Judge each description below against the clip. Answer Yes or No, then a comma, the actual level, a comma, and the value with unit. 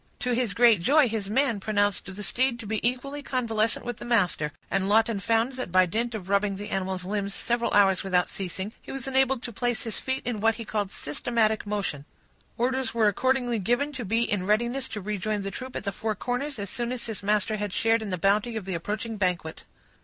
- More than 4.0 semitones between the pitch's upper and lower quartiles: No, average, 3.4 semitones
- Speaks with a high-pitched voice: Yes, high, 220 Hz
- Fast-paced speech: Yes, fast, 220 wpm